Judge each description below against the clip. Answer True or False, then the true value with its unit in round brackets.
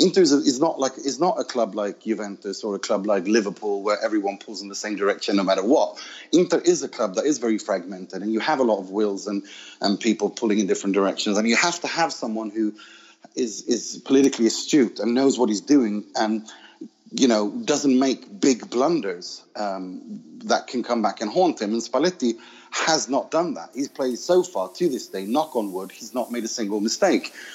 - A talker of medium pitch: False (115 Hz)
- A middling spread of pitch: False (5.9 semitones)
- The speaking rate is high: True (225 wpm)